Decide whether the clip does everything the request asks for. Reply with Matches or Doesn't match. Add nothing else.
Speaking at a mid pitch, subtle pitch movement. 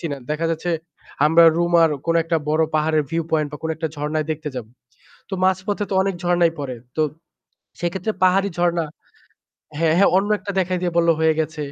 Matches